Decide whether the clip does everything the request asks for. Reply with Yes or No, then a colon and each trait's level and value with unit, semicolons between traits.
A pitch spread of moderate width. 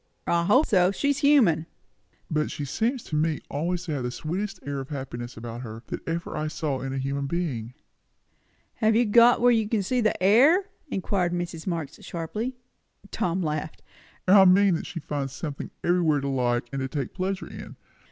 No: wide, 6.2 semitones